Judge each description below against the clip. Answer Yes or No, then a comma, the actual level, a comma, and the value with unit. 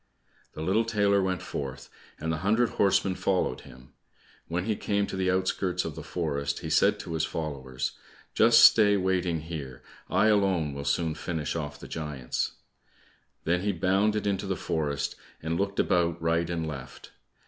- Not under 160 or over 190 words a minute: Yes, average, 170 wpm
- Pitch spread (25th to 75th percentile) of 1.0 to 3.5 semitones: No, average, 4.3 semitones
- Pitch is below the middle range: Yes, very low, 85 Hz